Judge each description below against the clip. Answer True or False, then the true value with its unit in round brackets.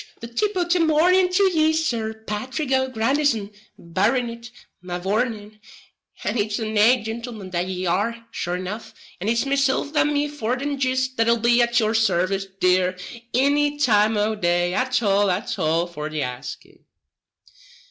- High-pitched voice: True (230 Hz)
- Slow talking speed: False (155 wpm)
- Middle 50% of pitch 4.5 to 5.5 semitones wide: True (5.2 semitones)